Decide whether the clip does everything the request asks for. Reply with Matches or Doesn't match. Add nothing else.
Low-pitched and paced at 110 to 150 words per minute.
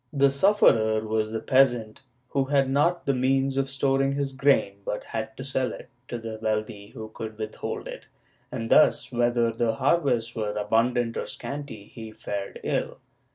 Doesn't match